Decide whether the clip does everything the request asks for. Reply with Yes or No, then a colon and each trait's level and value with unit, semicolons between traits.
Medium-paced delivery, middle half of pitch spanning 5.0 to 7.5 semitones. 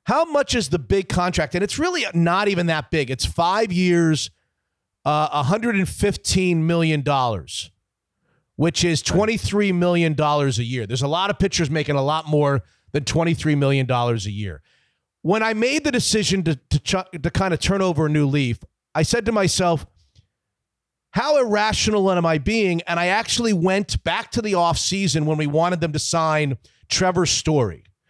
Yes: average, 170 wpm; average, 5.3 semitones